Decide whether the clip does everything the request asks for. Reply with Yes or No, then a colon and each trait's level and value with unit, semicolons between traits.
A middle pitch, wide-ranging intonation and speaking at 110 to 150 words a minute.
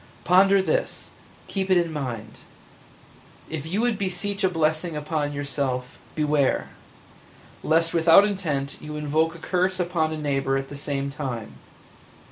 No: medium, 155 Hz; average, 4.2 semitones; average, 145 wpm